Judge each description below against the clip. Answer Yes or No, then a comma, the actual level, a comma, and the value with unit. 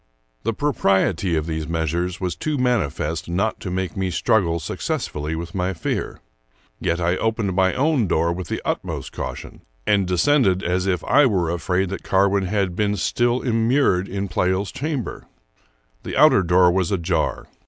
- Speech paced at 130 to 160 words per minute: No, average, 170 wpm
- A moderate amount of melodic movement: Yes, average, 3.3 semitones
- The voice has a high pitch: No, very low, 95 Hz